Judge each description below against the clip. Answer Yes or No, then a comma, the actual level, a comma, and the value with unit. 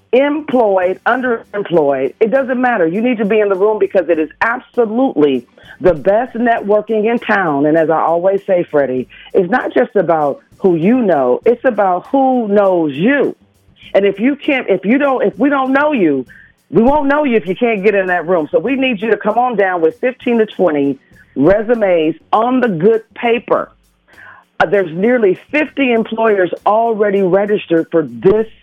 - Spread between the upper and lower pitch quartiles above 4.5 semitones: Yes, average, 5.1 semitones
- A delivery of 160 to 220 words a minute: Yes, average, 185 wpm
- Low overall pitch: No, high, 210 Hz